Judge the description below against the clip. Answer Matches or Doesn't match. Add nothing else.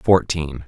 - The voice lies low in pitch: Matches